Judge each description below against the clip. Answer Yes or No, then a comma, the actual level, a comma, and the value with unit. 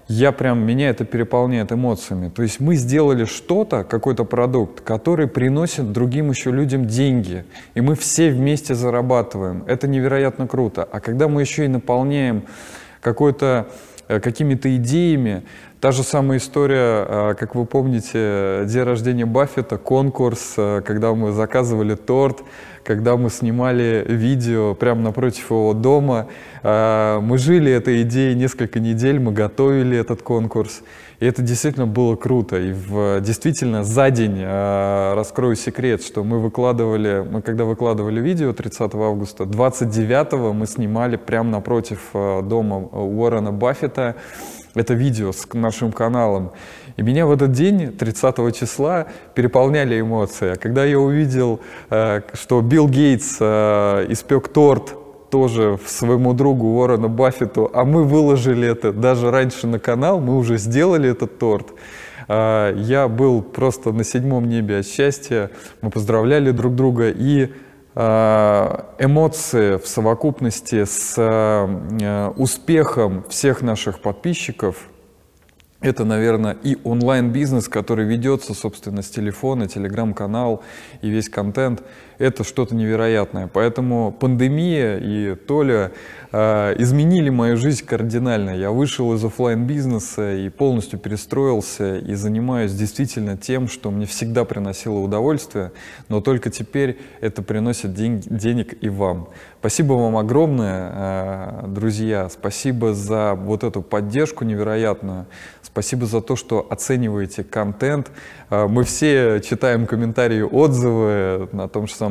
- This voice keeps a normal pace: Yes, average, 125 wpm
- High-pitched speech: No, low, 115 Hz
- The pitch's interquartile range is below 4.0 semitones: Yes, average, 3.6 semitones